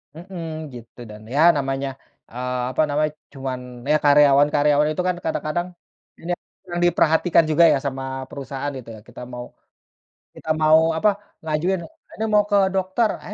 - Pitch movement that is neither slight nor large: Yes, average, 4.3 semitones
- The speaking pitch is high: No, medium, 150 Hz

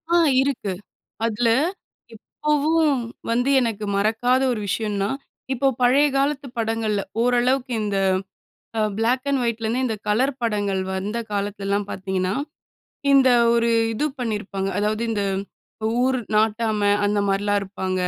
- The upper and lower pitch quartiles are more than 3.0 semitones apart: Yes, average, 3.7 semitones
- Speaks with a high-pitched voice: Yes, high, 225 Hz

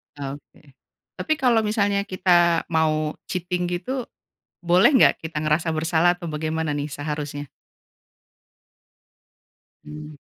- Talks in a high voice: No, medium, 160 Hz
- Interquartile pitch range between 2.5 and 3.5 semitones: Yes, average, 3.0 semitones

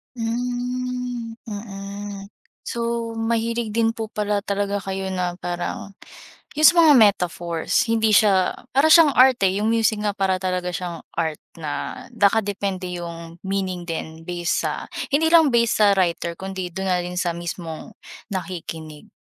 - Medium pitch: No, high, 200 Hz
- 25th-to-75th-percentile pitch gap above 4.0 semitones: Yes, average, 4.4 semitones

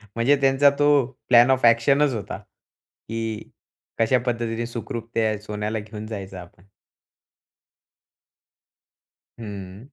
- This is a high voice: No, low, 115 Hz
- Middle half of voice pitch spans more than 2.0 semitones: Yes, narrow, 2.5 semitones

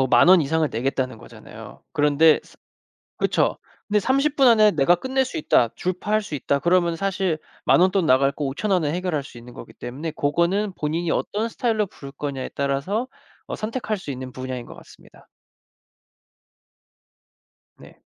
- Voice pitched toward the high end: No, medium, 165 Hz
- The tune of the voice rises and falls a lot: Yes, wide, 6.8 semitones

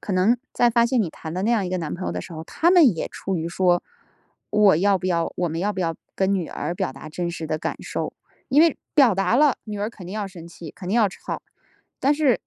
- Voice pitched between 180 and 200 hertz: Yes, high, 190 Hz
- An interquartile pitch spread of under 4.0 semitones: No, average, 5.1 semitones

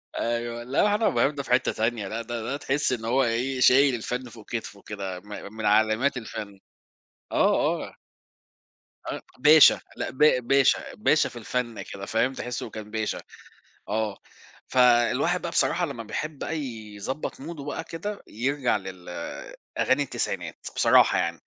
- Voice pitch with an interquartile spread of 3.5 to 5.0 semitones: Yes, average, 3.9 semitones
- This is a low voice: Yes, low, 120 Hz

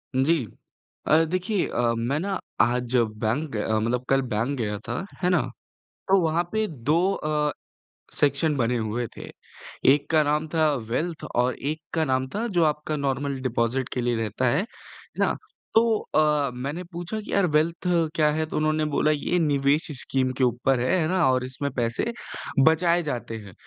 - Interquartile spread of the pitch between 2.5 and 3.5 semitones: No, average, 4.5 semitones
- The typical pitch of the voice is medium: Yes, medium, 145 Hz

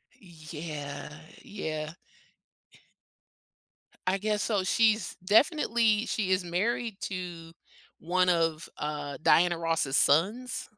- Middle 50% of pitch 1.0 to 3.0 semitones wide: No, average, 4.9 semitones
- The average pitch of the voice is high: No, medium, 180 Hz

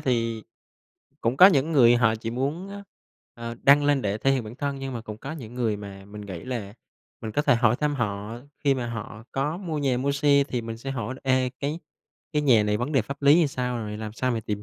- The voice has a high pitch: No, low, 125 Hz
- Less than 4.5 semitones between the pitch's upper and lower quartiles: Yes, average, 4.1 semitones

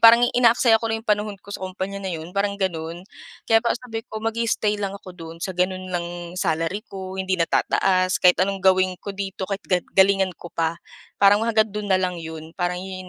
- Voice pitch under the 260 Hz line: Yes, high, 190 Hz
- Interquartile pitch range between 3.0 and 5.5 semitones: No, narrow, 2.5 semitones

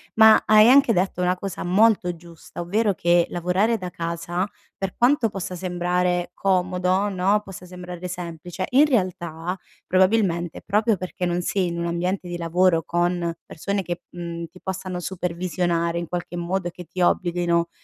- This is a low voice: No, medium, 180 Hz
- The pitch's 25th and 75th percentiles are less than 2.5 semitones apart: Yes, narrow, 1.8 semitones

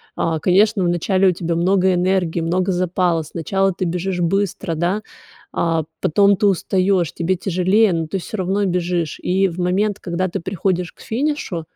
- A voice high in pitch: No, medium, 180 Hz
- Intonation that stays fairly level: Yes, narrow, 2.2 semitones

